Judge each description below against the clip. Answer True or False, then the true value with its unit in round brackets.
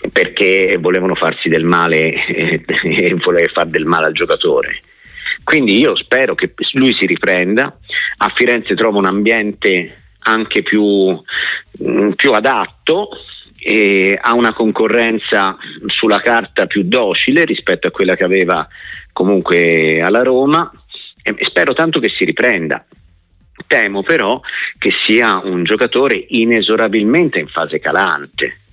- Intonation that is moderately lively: True (4.5 semitones)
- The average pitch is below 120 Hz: True (110 Hz)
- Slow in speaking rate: False (125 wpm)